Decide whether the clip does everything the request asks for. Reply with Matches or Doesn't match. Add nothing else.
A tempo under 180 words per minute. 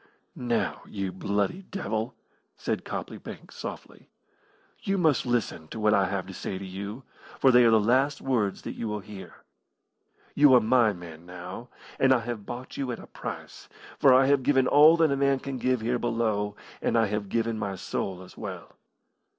Doesn't match